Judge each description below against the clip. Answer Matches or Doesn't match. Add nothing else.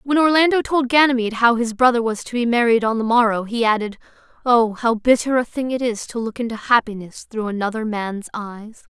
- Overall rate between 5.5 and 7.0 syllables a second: Matches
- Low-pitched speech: Doesn't match